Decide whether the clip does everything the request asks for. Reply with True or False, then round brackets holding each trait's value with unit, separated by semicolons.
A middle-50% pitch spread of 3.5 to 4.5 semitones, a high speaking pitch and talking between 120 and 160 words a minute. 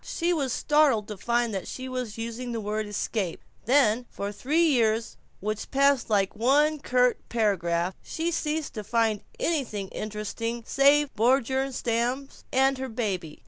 True (4.2 semitones; 235 Hz; 150 wpm)